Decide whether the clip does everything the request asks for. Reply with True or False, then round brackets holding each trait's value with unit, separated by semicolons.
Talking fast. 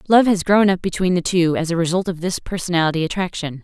True (230 wpm)